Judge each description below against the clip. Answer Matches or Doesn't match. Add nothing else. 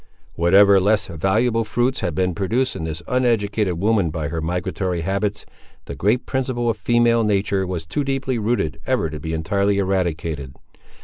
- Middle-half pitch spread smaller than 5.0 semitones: Doesn't match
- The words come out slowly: Doesn't match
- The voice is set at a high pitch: Doesn't match